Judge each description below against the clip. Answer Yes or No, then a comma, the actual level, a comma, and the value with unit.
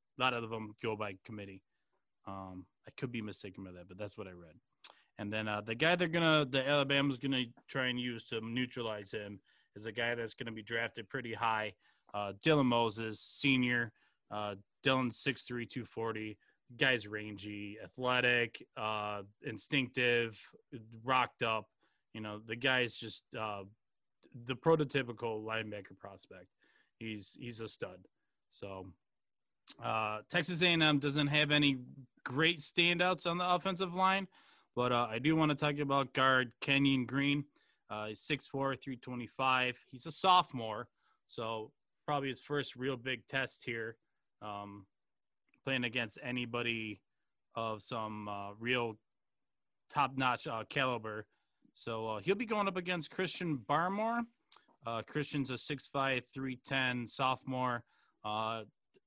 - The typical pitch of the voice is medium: No, low, 120 Hz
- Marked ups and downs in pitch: No, average, 4.2 semitones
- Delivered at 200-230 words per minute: No, average, 145 wpm